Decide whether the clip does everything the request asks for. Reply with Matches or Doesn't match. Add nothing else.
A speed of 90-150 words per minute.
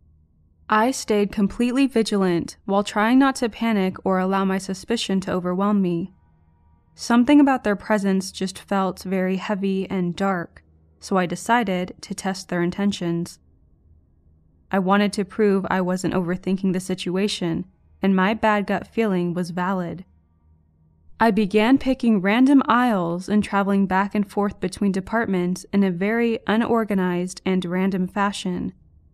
Matches